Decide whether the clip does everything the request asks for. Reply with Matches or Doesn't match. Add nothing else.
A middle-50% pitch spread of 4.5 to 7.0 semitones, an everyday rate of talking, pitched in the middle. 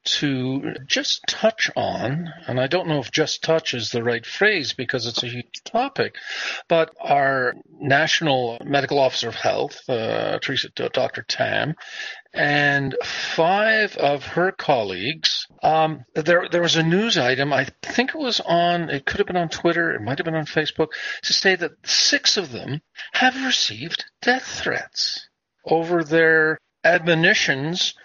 Matches